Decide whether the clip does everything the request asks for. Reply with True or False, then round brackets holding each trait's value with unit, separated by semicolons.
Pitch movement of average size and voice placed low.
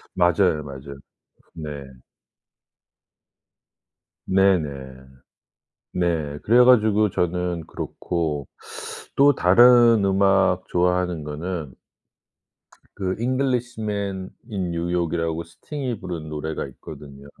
True (4.5 semitones; 90 Hz)